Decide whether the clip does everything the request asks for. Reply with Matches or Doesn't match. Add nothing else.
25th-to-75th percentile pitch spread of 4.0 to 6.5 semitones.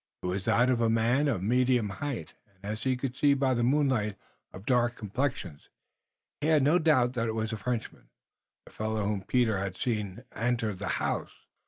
Doesn't match